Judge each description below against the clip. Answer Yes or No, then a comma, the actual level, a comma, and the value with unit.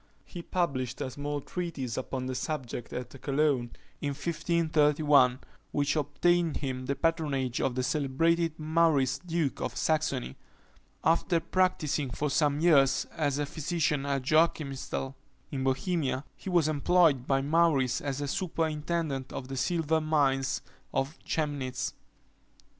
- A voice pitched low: No, medium, 145 Hz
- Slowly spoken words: Yes, slow, 130 wpm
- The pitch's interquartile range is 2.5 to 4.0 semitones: Yes, average, 3.3 semitones